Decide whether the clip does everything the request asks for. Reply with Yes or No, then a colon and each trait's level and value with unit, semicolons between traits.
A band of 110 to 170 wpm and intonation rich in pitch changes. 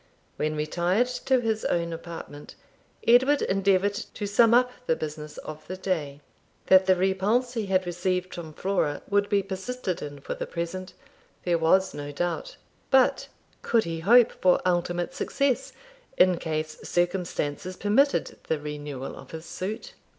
No: average, 150 wpm; average, 4.0 semitones